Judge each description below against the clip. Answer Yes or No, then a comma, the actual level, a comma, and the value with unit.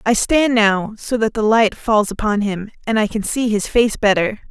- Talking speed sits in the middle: No, fast, 225 wpm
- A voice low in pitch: No, high, 215 Hz